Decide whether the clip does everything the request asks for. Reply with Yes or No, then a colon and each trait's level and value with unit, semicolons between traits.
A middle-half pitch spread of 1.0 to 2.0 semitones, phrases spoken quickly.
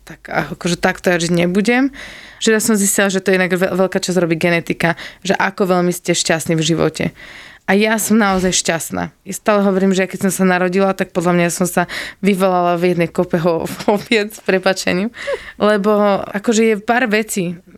No: narrow, 2.5 semitones; fast, 190 wpm